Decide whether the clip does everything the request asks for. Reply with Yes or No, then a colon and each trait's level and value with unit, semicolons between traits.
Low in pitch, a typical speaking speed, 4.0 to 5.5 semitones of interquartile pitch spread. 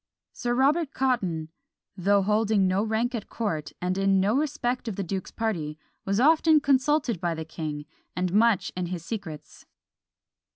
No: high, 205 Hz; average, 160 wpm; average, 5.2 semitones